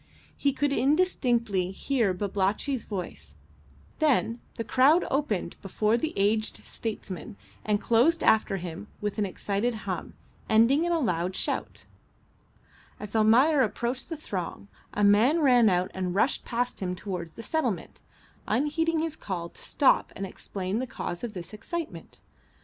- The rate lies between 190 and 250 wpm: No, average, 145 wpm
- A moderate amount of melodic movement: No, wide, 6.1 semitones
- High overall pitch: Yes, high, 220 Hz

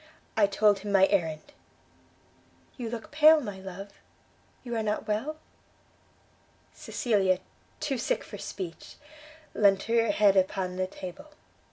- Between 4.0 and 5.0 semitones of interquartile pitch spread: No, average, 3.6 semitones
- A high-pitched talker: Yes, high, 205 Hz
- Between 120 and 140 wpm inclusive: Yes, slow, 135 wpm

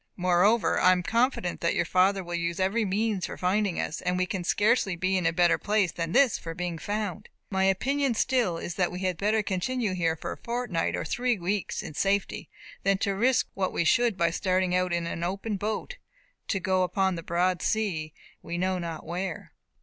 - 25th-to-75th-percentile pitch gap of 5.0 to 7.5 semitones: No, average, 3.2 semitones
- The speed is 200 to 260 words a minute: Yes, fast, 205 wpm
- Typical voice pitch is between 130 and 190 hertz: Yes, medium, 185 Hz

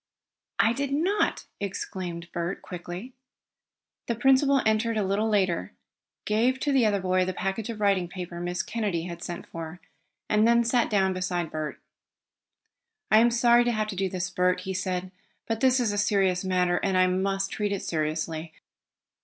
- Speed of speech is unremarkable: Yes, average, 175 wpm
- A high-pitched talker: Yes, high, 195 Hz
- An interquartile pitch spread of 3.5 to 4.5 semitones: Yes, average, 3.9 semitones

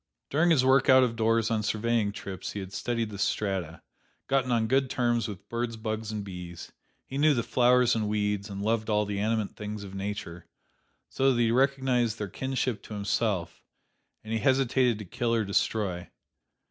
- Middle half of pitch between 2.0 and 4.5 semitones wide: Yes, average, 3.2 semitones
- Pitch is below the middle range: Yes, low, 110 Hz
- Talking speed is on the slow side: No, average, 185 wpm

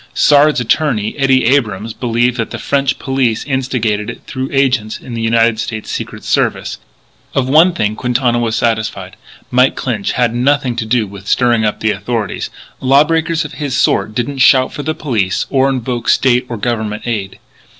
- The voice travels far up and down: No, average, 3.4 semitones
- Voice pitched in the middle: No, low, 125 Hz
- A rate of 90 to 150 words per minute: No, average, 175 wpm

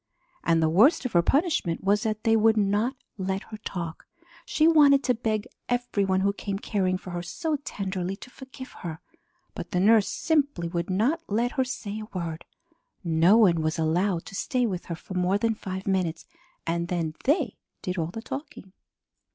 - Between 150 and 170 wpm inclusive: No, average, 190 wpm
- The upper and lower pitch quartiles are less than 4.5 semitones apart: No, average, 5.3 semitones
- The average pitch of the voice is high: Yes, high, 200 Hz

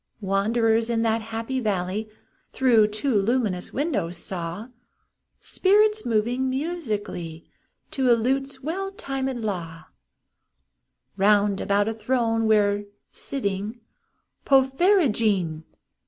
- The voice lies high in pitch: Yes, high, 225 Hz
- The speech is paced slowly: Yes, slow, 95 wpm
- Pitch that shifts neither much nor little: Yes, average, 4.6 semitones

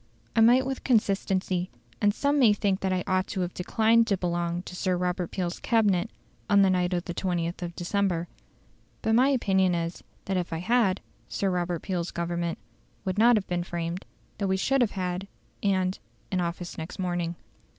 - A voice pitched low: No, medium, 185 Hz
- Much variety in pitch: No, average, 2.7 semitones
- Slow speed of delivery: No, average, 190 wpm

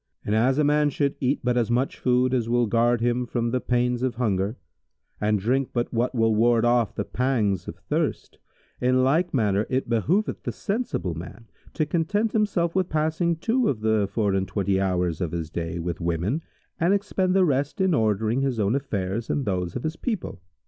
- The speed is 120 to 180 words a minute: No, average, 200 wpm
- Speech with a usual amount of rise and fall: No, wide, 5.9 semitones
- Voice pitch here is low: Yes, low, 120 Hz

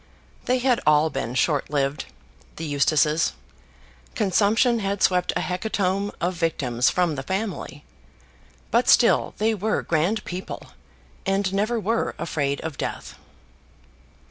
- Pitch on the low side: No, medium, 185 Hz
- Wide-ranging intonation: Yes, wide, 5.9 semitones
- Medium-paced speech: No, slow, 125 wpm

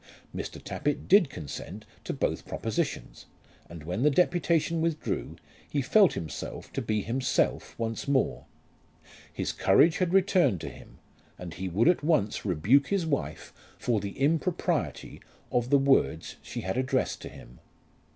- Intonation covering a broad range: Yes, wide, 8.7 semitones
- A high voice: No, low, 135 Hz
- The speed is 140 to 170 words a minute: Yes, average, 150 wpm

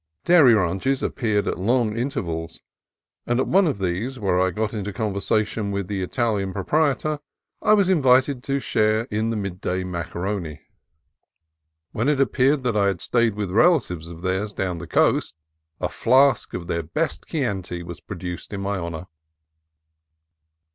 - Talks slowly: No, average, 160 wpm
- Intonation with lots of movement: Yes, wide, 5.7 semitones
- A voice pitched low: Yes, low, 105 Hz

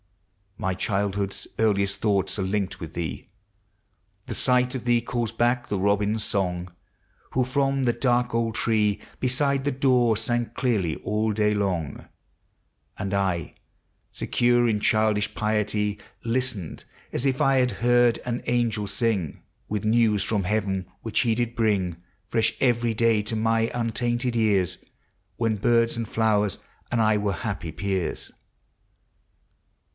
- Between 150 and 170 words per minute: No, average, 140 wpm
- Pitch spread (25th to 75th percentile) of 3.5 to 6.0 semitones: No, average, 3.0 semitones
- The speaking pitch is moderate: No, low, 110 Hz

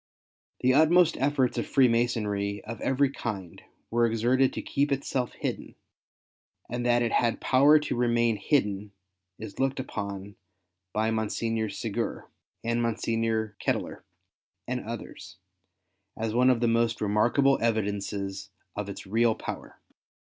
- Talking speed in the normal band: No, slow, 130 wpm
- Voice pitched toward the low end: Yes, low, 115 Hz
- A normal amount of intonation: Yes, average, 3.3 semitones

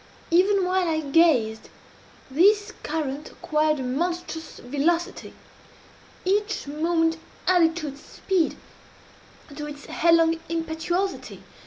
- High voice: Yes, very high, 325 Hz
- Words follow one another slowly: Yes, slow, 105 wpm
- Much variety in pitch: No, average, 3.0 semitones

